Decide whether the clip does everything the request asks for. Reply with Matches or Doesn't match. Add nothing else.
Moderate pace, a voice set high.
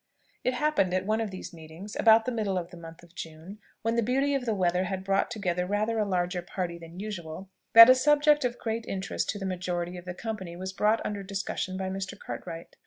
Doesn't match